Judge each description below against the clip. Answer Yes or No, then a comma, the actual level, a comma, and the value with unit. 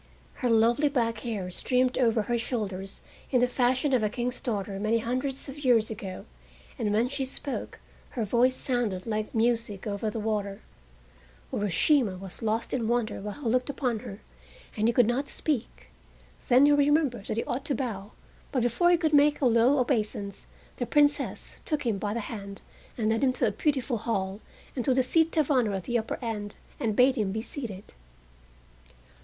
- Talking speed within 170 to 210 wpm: Yes, average, 190 wpm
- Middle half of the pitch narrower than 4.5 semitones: Yes, average, 3.5 semitones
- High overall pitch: Yes, high, 235 Hz